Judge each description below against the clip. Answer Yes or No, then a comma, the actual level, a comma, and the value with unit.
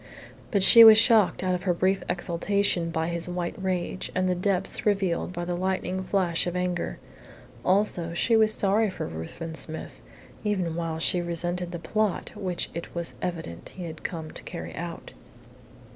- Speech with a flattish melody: Yes, narrow, 2.3 semitones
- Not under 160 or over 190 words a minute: Yes, average, 175 wpm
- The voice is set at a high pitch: No, medium, 180 Hz